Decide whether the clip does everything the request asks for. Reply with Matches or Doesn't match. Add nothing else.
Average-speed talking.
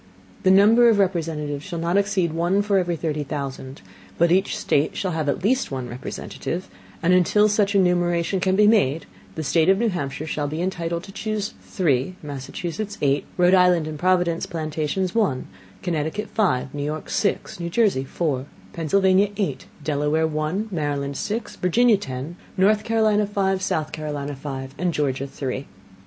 Matches